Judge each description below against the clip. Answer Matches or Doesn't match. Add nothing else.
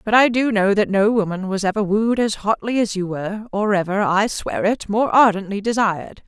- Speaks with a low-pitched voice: Doesn't match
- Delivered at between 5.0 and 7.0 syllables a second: Matches